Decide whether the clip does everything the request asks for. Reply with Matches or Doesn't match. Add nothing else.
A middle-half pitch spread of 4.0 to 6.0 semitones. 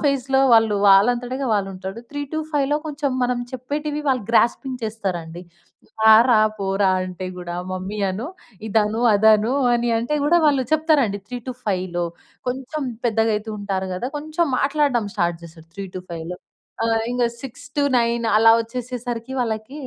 Matches